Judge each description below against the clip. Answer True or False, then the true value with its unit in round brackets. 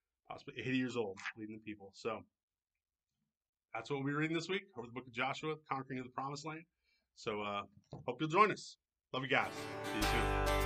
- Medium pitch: False (130 Hz)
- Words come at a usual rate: False (210 wpm)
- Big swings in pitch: True (6.1 semitones)